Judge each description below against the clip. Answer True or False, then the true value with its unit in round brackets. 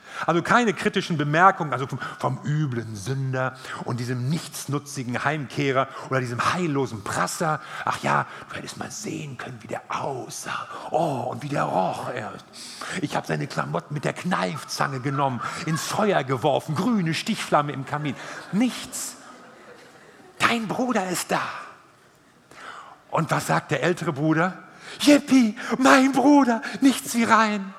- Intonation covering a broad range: True (7.7 semitones)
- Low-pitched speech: False (160 Hz)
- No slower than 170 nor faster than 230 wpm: False (140 wpm)